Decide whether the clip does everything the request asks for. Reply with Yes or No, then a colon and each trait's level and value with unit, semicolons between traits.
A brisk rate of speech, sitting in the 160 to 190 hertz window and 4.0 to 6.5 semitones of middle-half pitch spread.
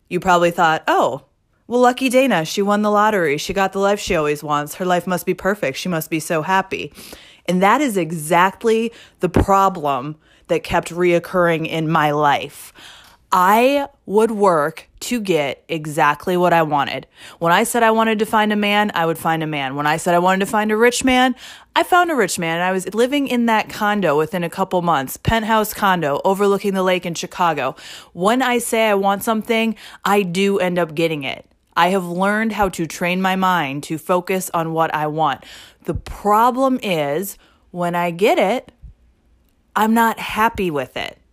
No: average, 195 wpm; medium, 185 Hz; average, 4.3 semitones